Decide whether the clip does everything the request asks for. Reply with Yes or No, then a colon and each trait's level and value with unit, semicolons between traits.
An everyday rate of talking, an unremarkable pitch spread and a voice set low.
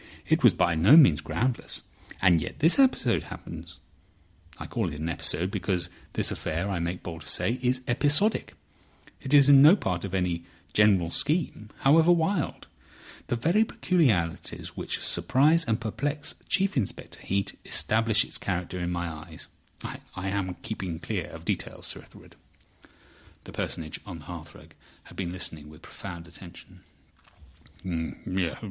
No: average, 145 wpm; wide, 8.4 semitones; low, 100 Hz